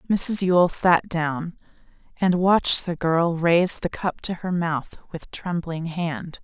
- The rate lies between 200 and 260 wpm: No, average, 160 wpm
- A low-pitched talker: No, medium, 170 Hz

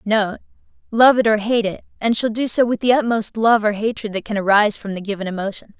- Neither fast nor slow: No, fast, 240 wpm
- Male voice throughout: No, female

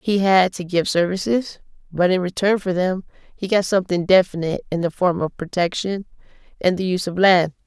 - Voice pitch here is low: No, medium, 185 Hz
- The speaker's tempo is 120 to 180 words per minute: No, average, 190 wpm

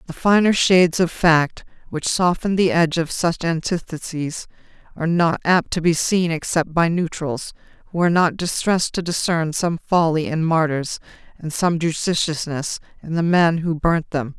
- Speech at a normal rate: Yes, average, 165 wpm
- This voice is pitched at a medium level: Yes, medium, 165 Hz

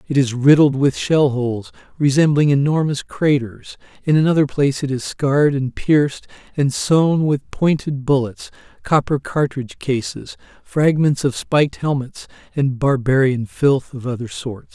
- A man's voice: Yes, male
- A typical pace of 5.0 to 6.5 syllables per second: No, 4.5 syllables/s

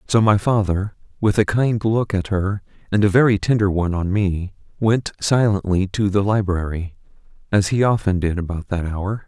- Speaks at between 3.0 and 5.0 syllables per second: Yes, 4.9 syllables/s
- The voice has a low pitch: Yes, low, 100 Hz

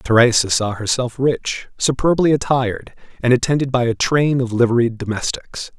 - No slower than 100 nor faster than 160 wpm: Yes, average, 145 wpm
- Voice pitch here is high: No, low, 125 Hz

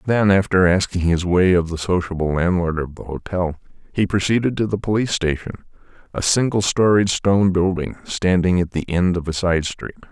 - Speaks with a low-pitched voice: Yes, very low, 90 Hz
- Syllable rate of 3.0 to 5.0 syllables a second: No, 5.4 syllables/s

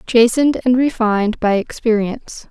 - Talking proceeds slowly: Yes, slow, 120 wpm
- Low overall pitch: No, high, 230 Hz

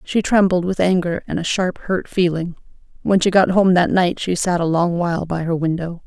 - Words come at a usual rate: No, fast, 230 wpm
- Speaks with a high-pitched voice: No, medium, 180 Hz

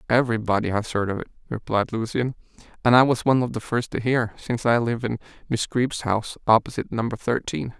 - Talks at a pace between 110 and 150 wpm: No, average, 200 wpm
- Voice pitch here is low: Yes, low, 115 Hz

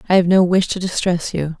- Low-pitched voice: No, medium, 180 Hz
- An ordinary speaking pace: No, fast, 265 wpm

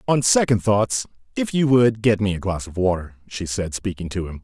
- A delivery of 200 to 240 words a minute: Yes, fast, 205 wpm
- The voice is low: Yes, low, 105 Hz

